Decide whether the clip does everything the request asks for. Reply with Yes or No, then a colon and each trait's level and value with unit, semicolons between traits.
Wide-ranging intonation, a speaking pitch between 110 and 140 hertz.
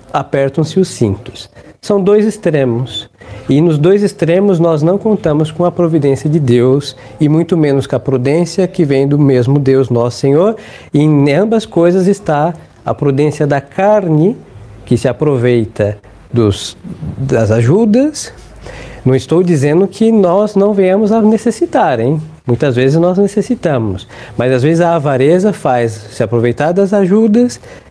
No: wide, 6.7 semitones; medium, 150 Hz